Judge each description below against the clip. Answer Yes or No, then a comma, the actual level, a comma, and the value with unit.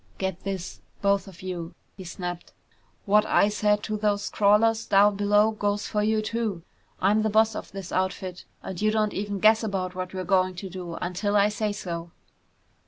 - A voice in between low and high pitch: No, high, 200 Hz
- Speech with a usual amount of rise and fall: No, narrow, 2.2 semitones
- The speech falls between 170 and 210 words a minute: Yes, average, 185 wpm